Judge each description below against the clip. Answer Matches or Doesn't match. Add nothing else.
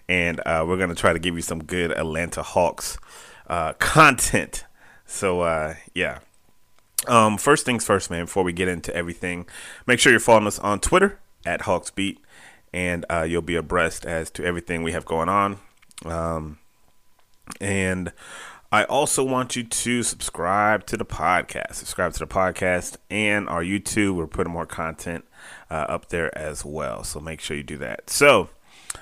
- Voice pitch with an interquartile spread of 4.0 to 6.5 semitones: Doesn't match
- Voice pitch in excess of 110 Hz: Doesn't match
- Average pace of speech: Matches